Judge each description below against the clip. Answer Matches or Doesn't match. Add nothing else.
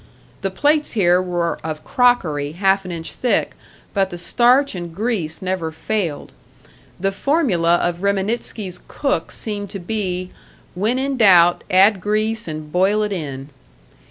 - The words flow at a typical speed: Matches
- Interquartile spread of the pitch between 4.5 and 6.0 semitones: Doesn't match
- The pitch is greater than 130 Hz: Matches